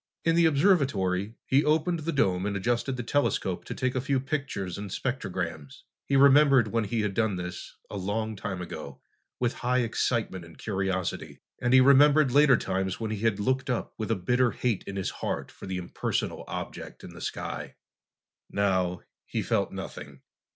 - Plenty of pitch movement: Yes, wide, 5.9 semitones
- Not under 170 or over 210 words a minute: Yes, average, 180 wpm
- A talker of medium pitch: No, low, 110 Hz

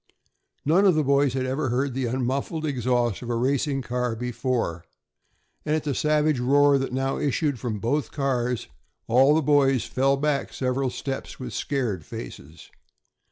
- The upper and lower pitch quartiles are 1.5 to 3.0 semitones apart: Yes, narrow, 2.6 semitones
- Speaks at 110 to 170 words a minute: Yes, average, 160 wpm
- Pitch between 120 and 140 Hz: Yes, low, 135 Hz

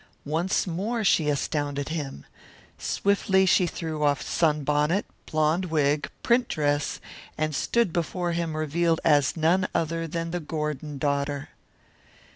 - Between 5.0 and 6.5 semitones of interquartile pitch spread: No, average, 2.8 semitones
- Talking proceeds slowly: Yes, slow, 125 wpm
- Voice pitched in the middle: Yes, medium, 155 Hz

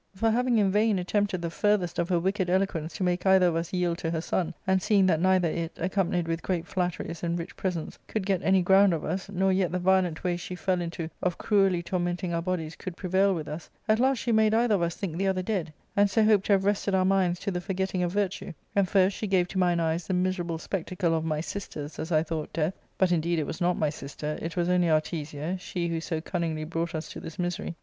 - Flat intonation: Yes, narrow, 2.3 semitones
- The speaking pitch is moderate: Yes, medium, 180 Hz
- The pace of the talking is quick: Yes, fast, 250 wpm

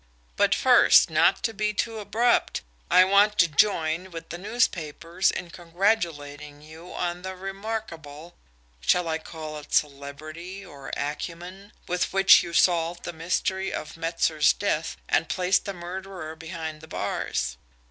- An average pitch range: Yes, average, 3.4 semitones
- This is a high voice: No, medium, 175 Hz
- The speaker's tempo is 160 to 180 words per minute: No, average, 145 wpm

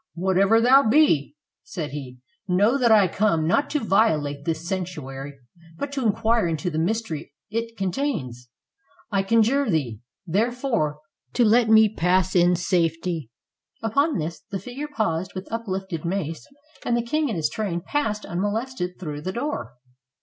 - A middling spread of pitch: No, wide, 5.8 semitones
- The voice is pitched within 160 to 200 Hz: Yes, high, 190 Hz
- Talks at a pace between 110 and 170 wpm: Yes, average, 150 wpm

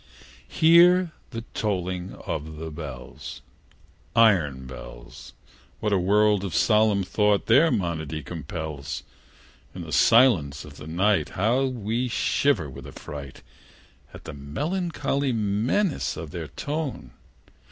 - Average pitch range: No, wide, 8.2 semitones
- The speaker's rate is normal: No, slow, 120 wpm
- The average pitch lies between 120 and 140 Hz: No, low, 100 Hz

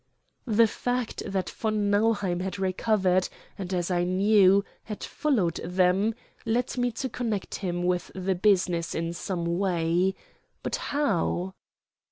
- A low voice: No, high, 190 Hz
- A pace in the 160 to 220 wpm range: No, slow, 135 wpm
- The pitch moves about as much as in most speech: Yes, average, 3.3 semitones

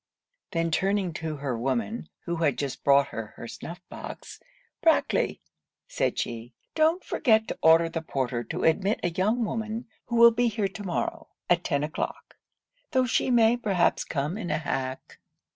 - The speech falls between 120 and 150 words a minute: No, average, 170 wpm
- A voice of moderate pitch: Yes, medium, 175 Hz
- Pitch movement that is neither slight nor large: No, wide, 7.7 semitones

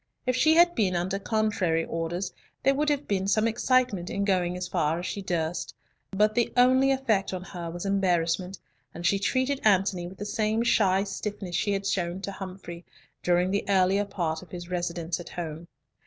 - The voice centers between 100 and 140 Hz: No, high, 190 Hz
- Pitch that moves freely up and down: No, average, 3.5 semitones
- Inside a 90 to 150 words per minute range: No, average, 190 wpm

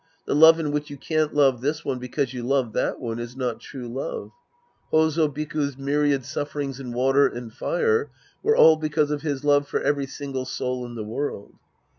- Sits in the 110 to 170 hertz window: Yes, medium, 140 Hz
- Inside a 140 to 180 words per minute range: No, average, 195 wpm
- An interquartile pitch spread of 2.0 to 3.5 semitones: Yes, average, 2.9 semitones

